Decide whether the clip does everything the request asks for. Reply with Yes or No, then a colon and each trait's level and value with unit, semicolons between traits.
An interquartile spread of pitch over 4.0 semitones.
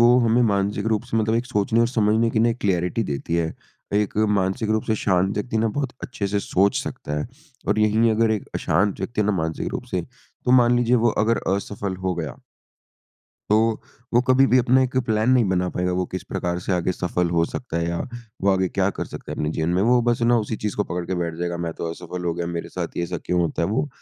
Yes: average, 4.4 semitones